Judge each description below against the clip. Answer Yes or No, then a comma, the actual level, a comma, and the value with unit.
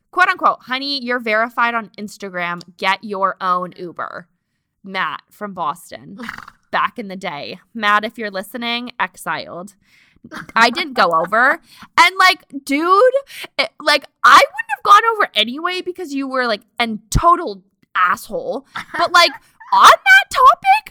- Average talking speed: Yes, average, 145 wpm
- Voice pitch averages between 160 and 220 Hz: No, high, 245 Hz